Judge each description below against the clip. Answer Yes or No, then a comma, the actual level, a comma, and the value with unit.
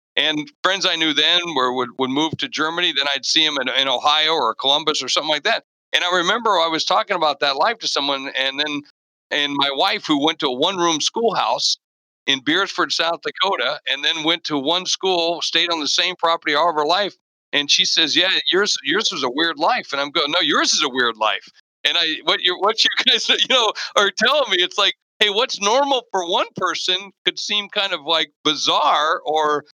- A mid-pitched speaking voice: Yes, medium, 165 Hz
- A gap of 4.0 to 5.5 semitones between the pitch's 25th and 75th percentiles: No, average, 3.6 semitones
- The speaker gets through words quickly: Yes, fast, 225 wpm